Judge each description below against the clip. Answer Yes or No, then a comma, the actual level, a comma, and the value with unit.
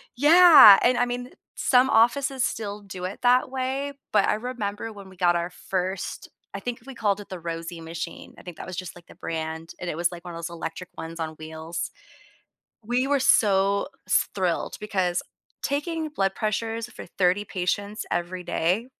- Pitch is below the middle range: No, high, 195 Hz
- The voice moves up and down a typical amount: No, wide, 5.8 semitones